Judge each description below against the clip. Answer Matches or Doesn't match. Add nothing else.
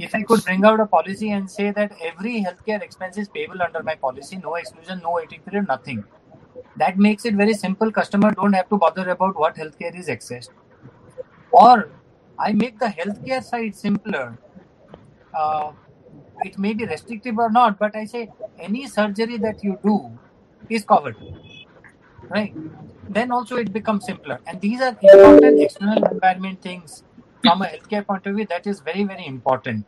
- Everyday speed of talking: Matches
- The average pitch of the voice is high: Matches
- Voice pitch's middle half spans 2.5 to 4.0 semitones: Doesn't match